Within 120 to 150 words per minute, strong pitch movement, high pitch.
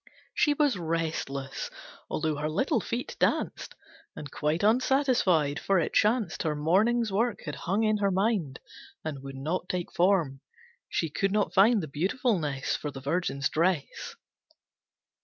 No: average, 145 wpm; wide, 6.0 semitones; medium, 175 Hz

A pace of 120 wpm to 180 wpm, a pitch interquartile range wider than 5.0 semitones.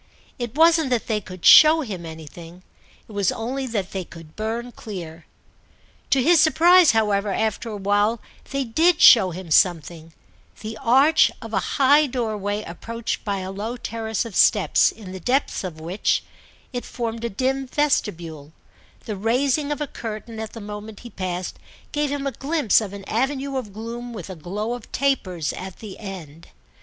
Yes: average, 170 wpm; wide, 5.4 semitones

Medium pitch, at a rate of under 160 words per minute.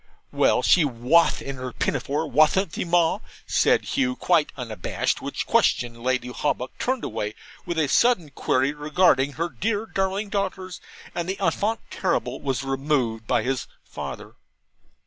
Yes: medium, 150 Hz; average, 145 wpm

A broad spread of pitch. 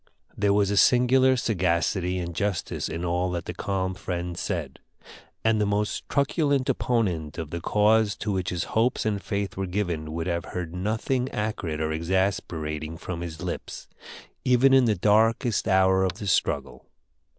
No: average, 4.0 semitones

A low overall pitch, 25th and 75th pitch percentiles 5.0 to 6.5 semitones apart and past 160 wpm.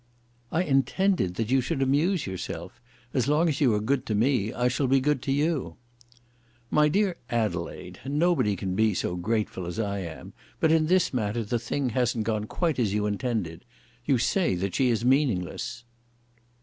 Yes: low, 125 Hz; wide, 5.6 semitones; average, 180 wpm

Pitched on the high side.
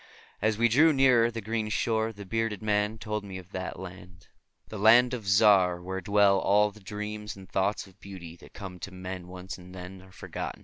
No: low, 100 Hz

